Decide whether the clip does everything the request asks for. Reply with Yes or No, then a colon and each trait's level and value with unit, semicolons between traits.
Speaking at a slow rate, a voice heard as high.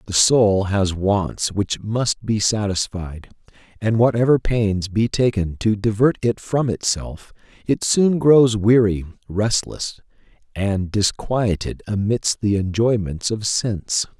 No: slow, 125 wpm; low, 105 Hz